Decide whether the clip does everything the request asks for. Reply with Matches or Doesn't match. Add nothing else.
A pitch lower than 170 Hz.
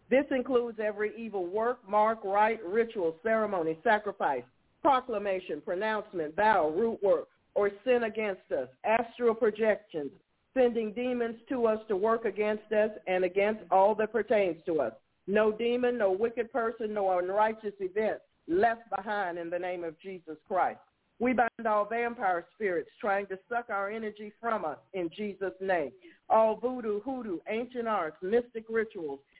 Doesn't match